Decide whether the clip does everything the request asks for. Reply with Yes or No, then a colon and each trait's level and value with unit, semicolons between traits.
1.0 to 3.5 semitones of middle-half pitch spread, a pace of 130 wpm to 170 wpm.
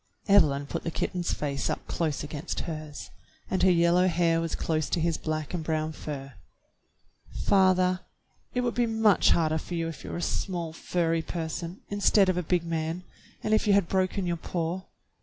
No: narrow, 2.6 semitones; average, 195 wpm